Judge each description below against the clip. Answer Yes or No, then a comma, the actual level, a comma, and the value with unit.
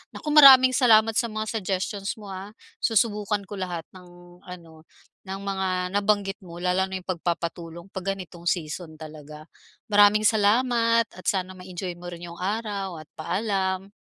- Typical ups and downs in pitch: Yes, average, 3.1 semitones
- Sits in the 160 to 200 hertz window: Yes, high, 190 Hz